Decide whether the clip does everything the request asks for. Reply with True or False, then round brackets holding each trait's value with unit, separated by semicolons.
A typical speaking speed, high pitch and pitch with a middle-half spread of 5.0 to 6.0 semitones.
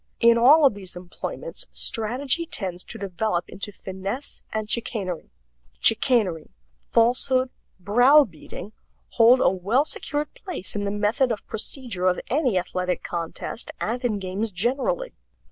False (130 wpm; 220 Hz; 5.4 semitones)